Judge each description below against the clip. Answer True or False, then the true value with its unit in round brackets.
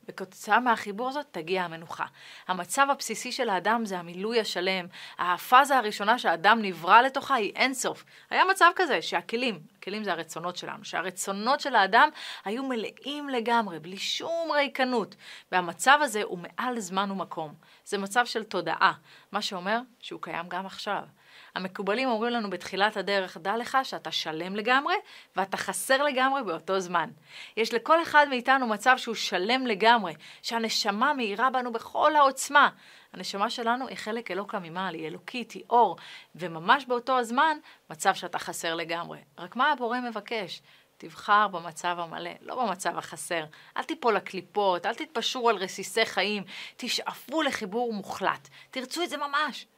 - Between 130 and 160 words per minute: True (145 wpm)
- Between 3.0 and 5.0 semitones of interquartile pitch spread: False (5.5 semitones)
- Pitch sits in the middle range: False (215 Hz)